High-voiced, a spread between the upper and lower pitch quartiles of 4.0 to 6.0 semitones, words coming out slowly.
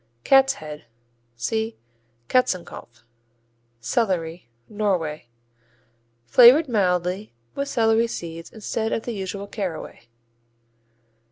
Yes: high, 200 Hz; wide, 5.4 semitones; slow, 85 wpm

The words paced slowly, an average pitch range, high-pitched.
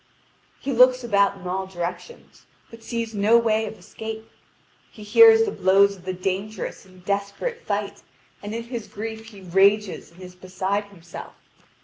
No: average, 160 wpm; average, 3.2 semitones; high, 205 Hz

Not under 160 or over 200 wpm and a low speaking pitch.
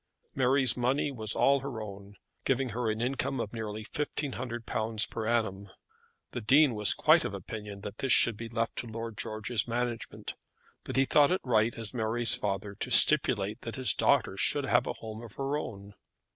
Yes: average, 185 wpm; low, 115 Hz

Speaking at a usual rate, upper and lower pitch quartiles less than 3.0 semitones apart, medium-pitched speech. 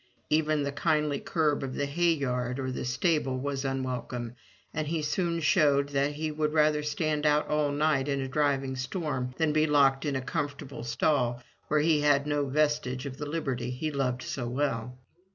Yes: average, 190 wpm; narrow, 2.5 semitones; medium, 145 Hz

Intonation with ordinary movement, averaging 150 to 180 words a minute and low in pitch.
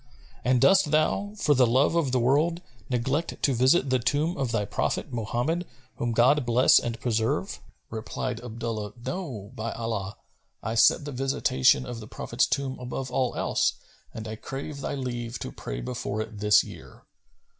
Yes: average, 3.6 semitones; average, 170 wpm; low, 125 Hz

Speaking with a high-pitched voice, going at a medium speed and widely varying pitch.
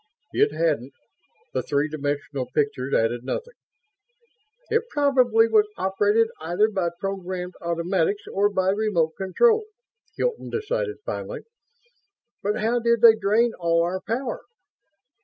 No: high, 195 Hz; slow, 120 wpm; wide, 5.7 semitones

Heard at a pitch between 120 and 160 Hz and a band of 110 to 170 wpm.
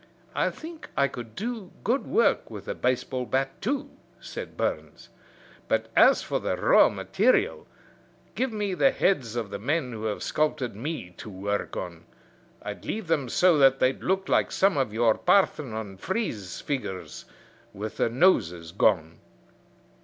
Yes: low, 135 Hz; average, 155 wpm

